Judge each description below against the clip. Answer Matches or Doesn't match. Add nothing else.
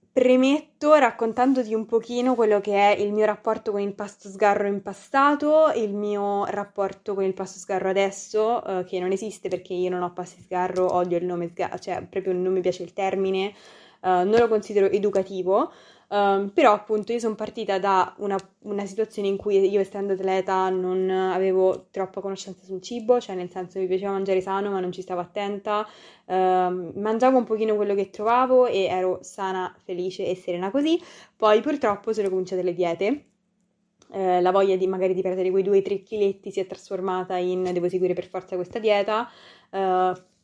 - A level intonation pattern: Matches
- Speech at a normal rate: Doesn't match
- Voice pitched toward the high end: Matches